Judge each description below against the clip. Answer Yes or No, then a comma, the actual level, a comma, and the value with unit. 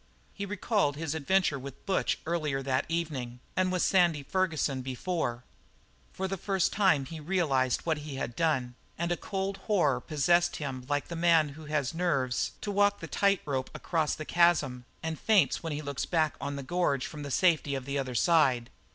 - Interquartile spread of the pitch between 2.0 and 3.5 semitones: No, average, 4.3 semitones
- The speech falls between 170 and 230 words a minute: Yes, average, 190 wpm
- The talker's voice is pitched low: No, medium, 155 Hz